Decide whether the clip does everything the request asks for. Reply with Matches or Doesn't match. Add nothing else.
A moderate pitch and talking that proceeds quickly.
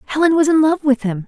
Doesn't match